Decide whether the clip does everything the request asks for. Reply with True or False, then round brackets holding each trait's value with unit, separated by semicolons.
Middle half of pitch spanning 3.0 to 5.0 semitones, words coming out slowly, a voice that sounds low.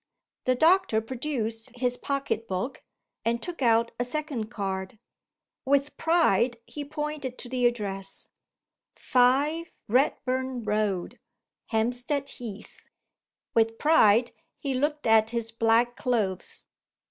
False (3.8 semitones; 110 wpm; 245 Hz)